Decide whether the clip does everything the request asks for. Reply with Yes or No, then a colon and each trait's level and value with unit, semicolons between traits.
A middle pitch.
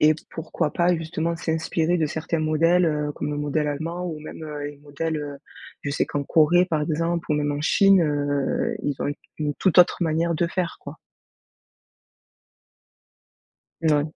Yes: medium, 155 Hz